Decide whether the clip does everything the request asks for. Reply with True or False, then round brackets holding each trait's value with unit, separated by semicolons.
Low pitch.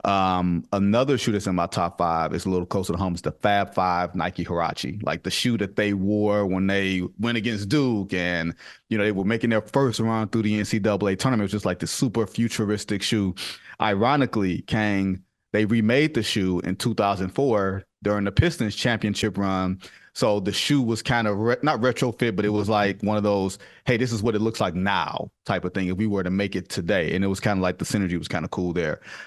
True (100 Hz)